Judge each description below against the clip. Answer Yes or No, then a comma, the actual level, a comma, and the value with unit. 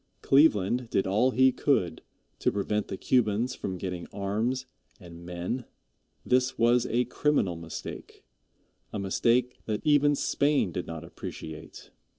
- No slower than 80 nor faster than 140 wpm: Yes, slow, 135 wpm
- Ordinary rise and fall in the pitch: No, wide, 5.7 semitones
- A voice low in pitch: Yes, low, 110 Hz